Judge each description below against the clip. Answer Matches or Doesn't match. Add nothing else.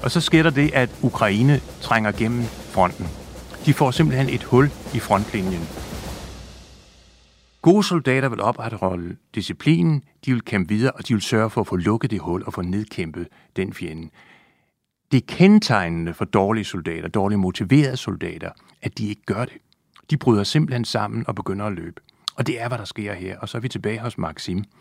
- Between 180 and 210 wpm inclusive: Matches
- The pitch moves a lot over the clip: Matches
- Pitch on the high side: Doesn't match